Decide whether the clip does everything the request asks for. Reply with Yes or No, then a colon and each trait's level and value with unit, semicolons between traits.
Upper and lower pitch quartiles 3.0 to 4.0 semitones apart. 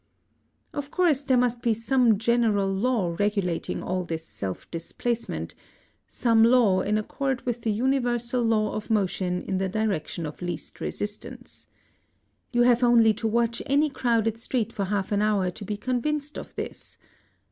Yes: average, 3.4 semitones